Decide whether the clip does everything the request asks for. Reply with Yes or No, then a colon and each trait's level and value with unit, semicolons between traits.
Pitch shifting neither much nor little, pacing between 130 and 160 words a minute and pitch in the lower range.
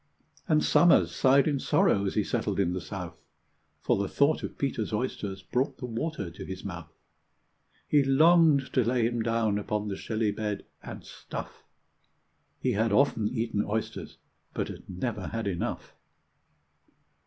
Yes: average, 5.0 semitones; average, 155 wpm; low, 110 Hz